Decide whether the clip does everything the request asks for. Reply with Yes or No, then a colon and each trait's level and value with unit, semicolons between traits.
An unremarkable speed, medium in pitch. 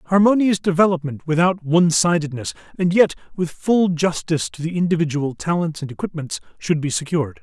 Yes: average, 155 wpm; medium, 165 Hz